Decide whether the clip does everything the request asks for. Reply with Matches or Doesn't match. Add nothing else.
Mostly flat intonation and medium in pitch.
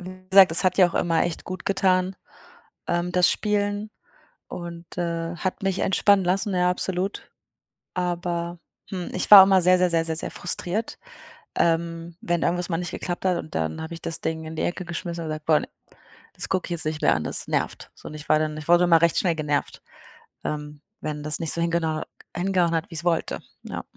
Matches